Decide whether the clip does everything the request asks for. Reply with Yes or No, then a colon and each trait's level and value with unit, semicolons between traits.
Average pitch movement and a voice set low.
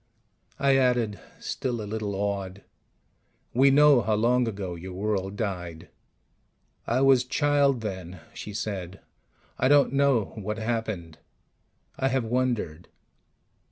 Yes: average, 4.8 semitones; low, 110 Hz